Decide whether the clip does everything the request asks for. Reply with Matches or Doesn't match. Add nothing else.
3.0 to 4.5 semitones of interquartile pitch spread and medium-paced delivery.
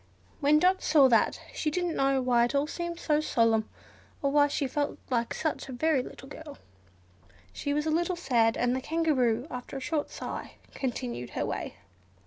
Matches